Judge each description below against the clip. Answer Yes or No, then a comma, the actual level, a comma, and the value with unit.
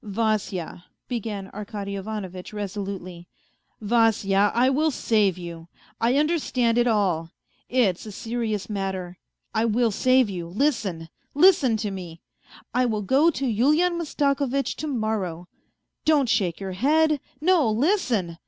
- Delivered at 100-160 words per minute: Yes, average, 140 wpm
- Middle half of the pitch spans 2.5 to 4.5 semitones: No, average, 5.3 semitones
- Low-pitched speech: No, high, 220 Hz